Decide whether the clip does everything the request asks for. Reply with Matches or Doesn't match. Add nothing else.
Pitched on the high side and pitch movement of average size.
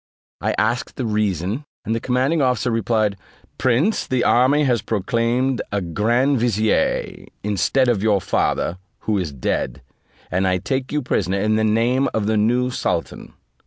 Doesn't match